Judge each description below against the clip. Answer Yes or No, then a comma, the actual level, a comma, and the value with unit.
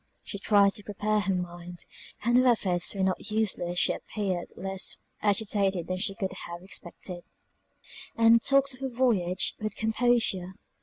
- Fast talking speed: No, average, 155 wpm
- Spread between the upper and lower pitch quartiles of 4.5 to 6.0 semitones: No, average, 3.4 semitones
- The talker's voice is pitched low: No, high, 200 Hz